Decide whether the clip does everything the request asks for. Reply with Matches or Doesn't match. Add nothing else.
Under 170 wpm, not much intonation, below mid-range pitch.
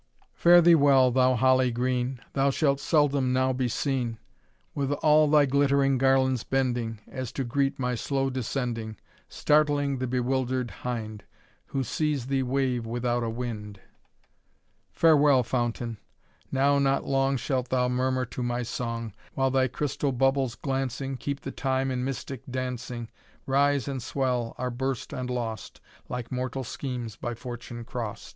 Matches